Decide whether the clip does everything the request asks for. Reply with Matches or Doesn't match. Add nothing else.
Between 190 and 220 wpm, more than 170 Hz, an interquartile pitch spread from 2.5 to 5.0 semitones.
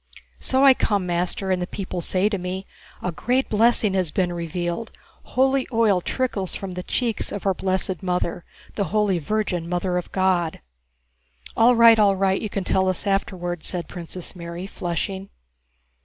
Doesn't match